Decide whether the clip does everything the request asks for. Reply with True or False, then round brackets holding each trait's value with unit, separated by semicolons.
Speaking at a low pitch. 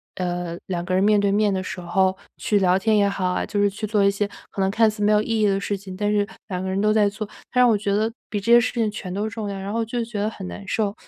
False (205 Hz)